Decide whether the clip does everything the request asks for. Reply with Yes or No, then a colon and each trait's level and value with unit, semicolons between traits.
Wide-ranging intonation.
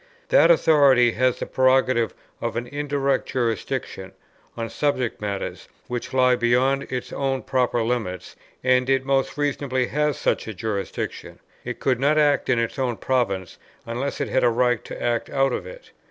No: narrow, 2.5 semitones